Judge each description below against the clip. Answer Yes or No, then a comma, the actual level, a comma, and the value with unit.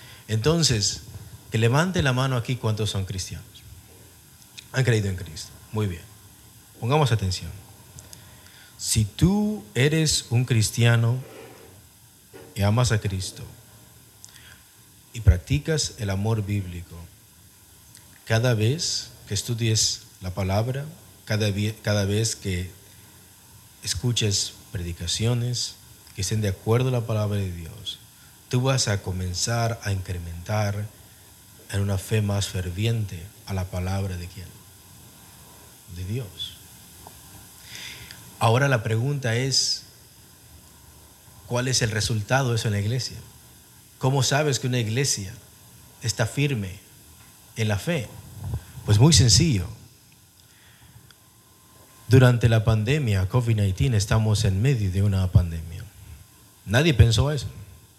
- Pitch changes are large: No, average, 3.3 semitones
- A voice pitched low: Yes, low, 110 Hz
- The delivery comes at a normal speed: No, slow, 115 wpm